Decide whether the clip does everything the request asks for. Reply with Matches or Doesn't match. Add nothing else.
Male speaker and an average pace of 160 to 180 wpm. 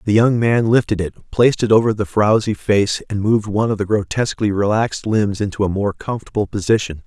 Doesn't match